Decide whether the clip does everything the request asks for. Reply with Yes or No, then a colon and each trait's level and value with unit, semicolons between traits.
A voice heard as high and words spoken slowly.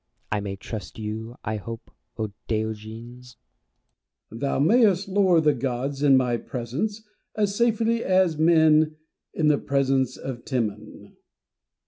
No: low, 135 Hz; slow, 130 wpm